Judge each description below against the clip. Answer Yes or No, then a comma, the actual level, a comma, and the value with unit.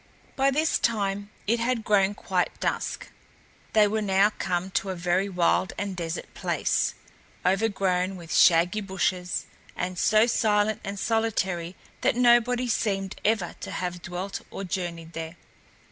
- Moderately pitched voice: No, high, 195 Hz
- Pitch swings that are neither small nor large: Yes, average, 3.3 semitones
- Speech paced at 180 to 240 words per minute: No, average, 145 wpm